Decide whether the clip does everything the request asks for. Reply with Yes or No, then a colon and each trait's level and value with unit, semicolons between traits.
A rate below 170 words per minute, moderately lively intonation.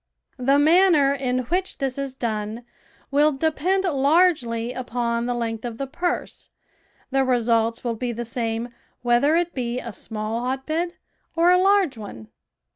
Yes: average, 150 wpm; average, 5.0 semitones